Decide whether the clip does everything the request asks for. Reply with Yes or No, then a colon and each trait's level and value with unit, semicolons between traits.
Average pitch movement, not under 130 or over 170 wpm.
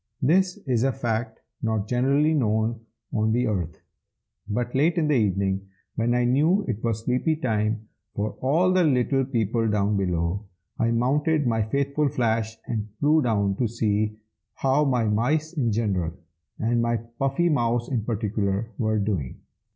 Yes: average, 4.1 semitones; average, 160 wpm